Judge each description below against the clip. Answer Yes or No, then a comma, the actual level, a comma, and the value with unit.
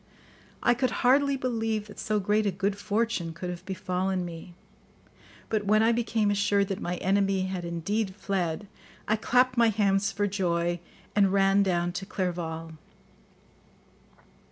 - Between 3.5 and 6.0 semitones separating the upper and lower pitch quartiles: No, average, 3.1 semitones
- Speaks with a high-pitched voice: Yes, high, 200 Hz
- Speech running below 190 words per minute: Yes, average, 150 wpm